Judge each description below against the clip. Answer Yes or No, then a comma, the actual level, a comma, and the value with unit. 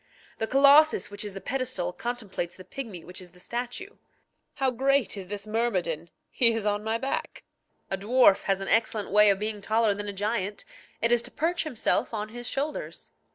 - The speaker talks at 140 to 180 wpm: No, average, 195 wpm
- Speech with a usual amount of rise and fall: Yes, average, 3.7 semitones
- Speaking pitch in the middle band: No, high, 220 Hz